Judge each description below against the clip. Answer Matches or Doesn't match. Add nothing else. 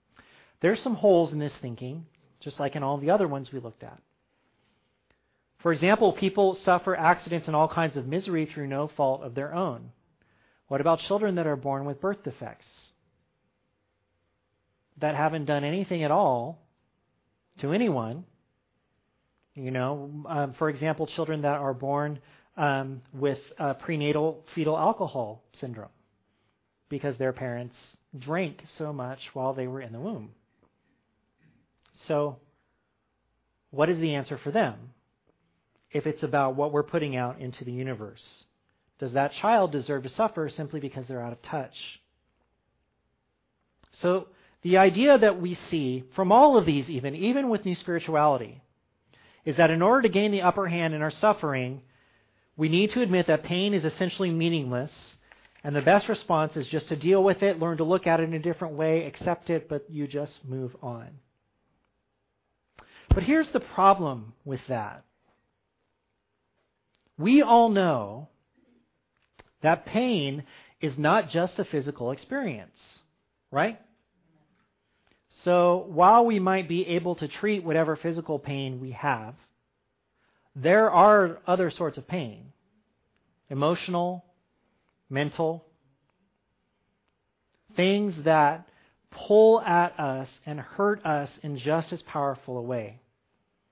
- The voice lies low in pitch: Doesn't match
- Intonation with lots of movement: Doesn't match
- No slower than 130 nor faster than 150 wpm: Matches